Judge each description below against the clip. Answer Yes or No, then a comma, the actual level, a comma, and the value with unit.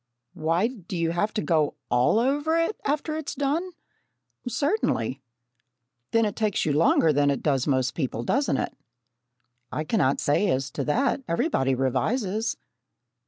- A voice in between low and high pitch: Yes, medium, 175 Hz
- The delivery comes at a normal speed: Yes, average, 155 wpm